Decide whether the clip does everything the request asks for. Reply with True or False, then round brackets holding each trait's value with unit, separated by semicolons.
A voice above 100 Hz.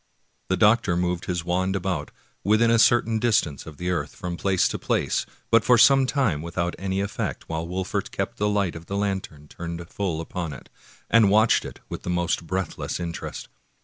False (95 Hz)